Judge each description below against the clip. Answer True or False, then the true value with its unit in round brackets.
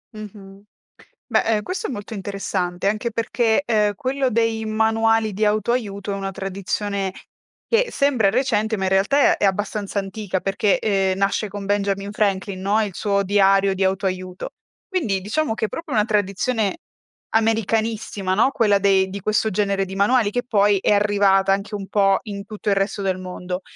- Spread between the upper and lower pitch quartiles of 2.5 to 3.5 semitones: False (2.1 semitones)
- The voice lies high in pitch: True (205 Hz)